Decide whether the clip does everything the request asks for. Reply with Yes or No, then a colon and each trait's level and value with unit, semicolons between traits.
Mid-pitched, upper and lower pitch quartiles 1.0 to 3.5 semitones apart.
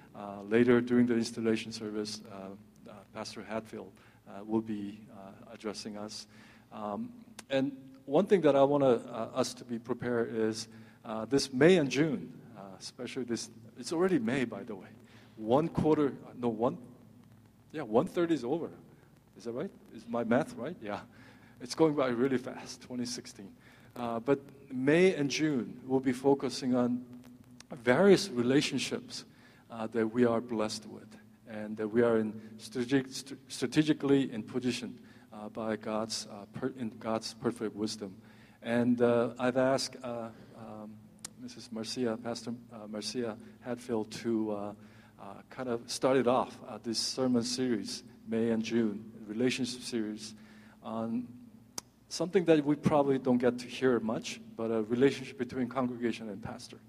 No: low, 120 Hz; narrow, 2.6 semitones